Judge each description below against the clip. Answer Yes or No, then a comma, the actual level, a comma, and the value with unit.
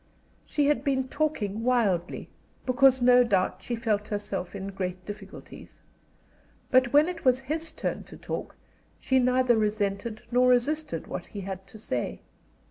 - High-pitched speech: Yes, high, 240 Hz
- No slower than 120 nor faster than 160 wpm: Yes, average, 150 wpm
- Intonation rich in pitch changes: No, average, 4.6 semitones